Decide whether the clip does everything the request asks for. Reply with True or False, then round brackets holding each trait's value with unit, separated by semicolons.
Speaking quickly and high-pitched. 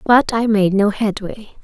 False (185 wpm; 210 Hz)